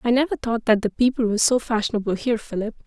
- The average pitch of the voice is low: No, high, 225 Hz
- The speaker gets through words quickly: Yes, fast, 230 wpm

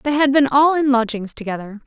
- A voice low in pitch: No, very high, 255 Hz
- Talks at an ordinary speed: No, fast, 225 wpm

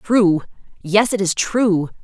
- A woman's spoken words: Yes, female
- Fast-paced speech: No, average, 150 wpm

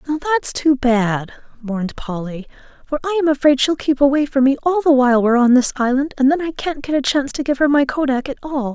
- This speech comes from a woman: Yes, female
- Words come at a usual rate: No, fast, 240 wpm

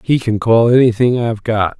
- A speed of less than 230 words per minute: Yes, average, 200 wpm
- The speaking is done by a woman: No, male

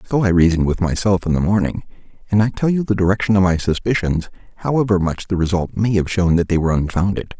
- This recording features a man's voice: Yes, male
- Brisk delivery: Yes, fast, 225 wpm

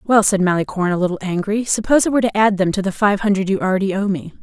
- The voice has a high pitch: Yes, high, 200 Hz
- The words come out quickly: Yes, fast, 270 wpm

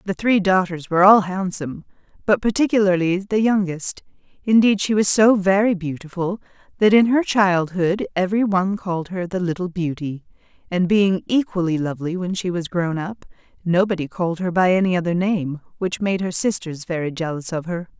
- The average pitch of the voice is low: No, medium, 185 Hz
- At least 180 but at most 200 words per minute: No, average, 170 wpm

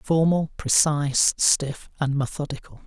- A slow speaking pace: Yes, slow, 105 wpm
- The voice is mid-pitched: Yes, medium, 145 Hz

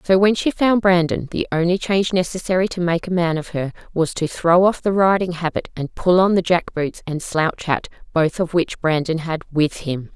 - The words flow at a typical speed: No, fast, 225 wpm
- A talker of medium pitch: Yes, medium, 175 Hz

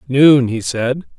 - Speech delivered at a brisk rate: No, average, 150 wpm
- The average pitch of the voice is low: Yes, low, 130 Hz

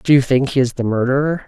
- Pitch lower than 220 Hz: Yes, low, 135 Hz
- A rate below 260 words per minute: No, fast, 285 wpm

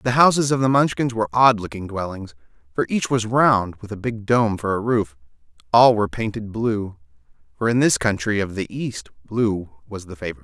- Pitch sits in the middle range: No, low, 110 Hz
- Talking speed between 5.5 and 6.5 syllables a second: Yes, 5.7 syllables/s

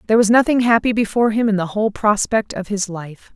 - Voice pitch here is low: No, high, 210 Hz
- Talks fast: Yes, fast, 230 wpm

